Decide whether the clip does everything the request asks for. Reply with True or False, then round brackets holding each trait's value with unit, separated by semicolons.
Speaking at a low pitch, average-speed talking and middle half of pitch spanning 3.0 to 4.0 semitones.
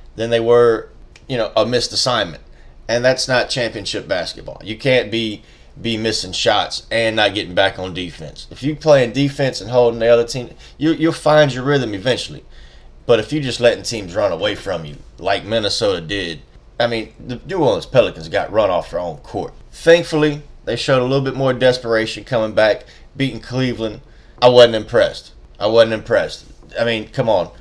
True (120 Hz; 190 wpm; 3.3 semitones)